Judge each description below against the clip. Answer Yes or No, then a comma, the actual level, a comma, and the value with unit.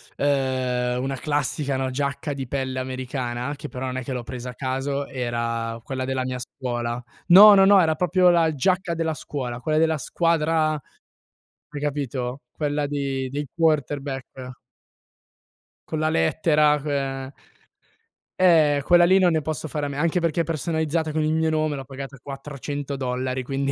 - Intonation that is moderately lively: Yes, average, 3.2 semitones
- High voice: No, medium, 140 Hz